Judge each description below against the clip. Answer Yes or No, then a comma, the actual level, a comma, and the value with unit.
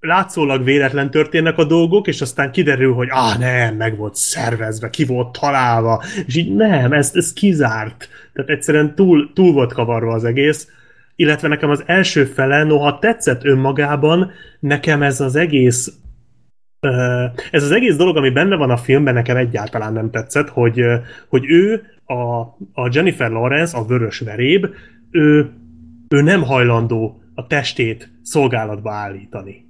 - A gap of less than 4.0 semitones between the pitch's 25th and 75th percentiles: No, average, 4.5 semitones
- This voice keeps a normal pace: Yes, average, 145 wpm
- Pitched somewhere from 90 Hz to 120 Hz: No, low, 135 Hz